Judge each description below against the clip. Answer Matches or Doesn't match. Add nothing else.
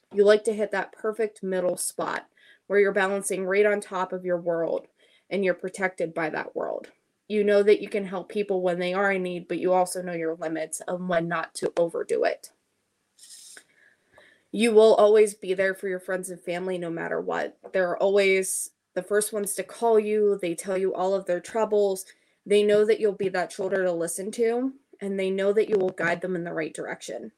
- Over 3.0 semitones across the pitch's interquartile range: Doesn't match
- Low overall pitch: Doesn't match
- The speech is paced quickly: Matches